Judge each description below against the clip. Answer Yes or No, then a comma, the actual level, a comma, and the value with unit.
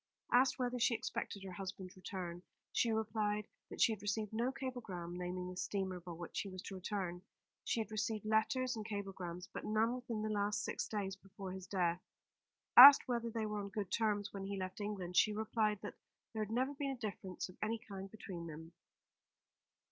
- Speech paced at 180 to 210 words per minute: Yes, average, 195 wpm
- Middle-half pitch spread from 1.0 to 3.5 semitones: Yes, average, 3.0 semitones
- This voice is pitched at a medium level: No, high, 205 Hz